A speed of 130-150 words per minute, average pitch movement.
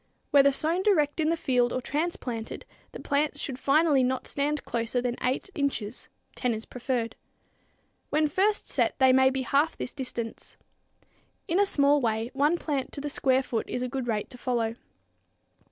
No: average, 175 wpm; average, 3.1 semitones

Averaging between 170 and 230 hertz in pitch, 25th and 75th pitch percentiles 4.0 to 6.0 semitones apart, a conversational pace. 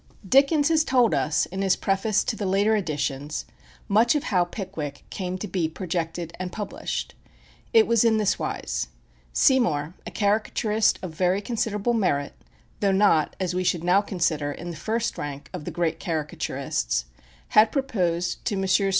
Yes: high, 190 Hz; average, 4.8 semitones; average, 165 wpm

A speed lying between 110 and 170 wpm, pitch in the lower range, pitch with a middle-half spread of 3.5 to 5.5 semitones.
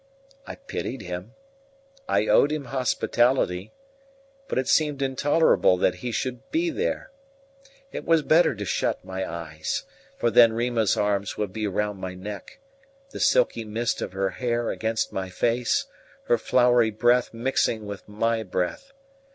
Yes: average, 150 wpm; low, 115 Hz; average, 4.2 semitones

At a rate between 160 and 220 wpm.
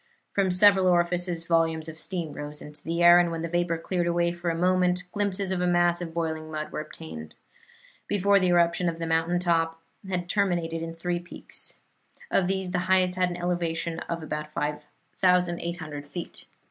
Yes: average, 180 wpm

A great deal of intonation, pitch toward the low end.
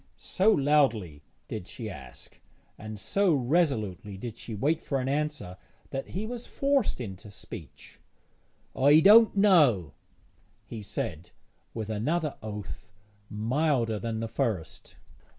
Yes: wide, 6.6 semitones; low, 120 Hz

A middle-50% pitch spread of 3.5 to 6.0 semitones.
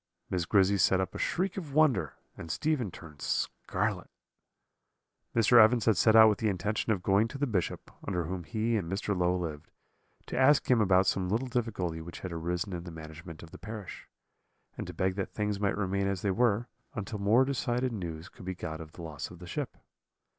Yes: average, 4.3 semitones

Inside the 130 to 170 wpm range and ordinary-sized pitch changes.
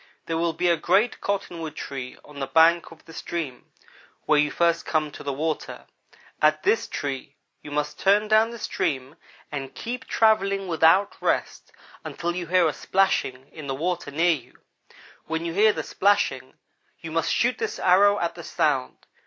No: average, 180 wpm; average, 4.6 semitones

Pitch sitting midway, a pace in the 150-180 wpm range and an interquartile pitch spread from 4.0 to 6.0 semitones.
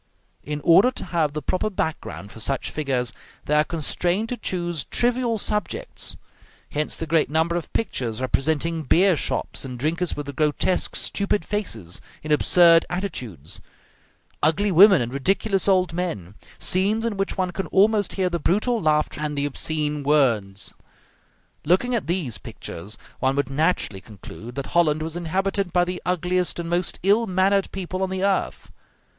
Yes: medium, 170 Hz; average, 160 wpm; average, 4.6 semitones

